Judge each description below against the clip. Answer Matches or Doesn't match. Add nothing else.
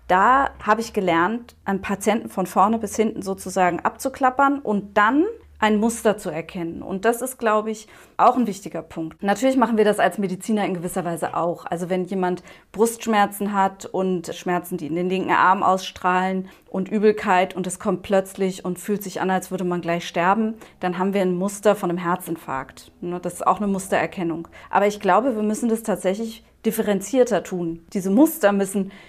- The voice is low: Doesn't match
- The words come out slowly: Doesn't match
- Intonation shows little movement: Doesn't match